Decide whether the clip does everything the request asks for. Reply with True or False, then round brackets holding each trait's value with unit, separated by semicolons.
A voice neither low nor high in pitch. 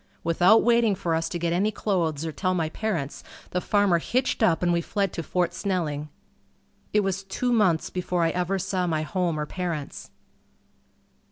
True (180 Hz)